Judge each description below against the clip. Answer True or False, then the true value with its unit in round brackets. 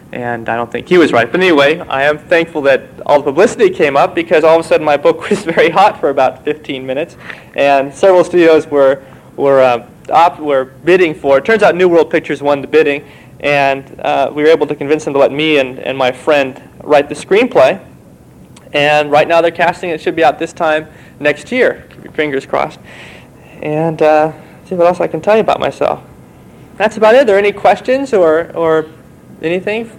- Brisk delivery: True (215 wpm)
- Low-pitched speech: False (155 Hz)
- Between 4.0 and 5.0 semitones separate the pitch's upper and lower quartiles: False (3.5 semitones)